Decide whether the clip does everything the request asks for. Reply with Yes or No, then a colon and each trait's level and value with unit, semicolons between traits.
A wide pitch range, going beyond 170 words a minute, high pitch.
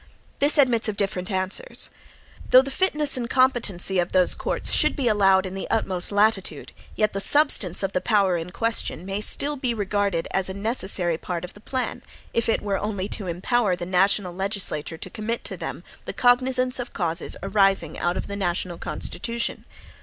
No: average, 4.3 semitones; average, 185 wpm; high, 200 Hz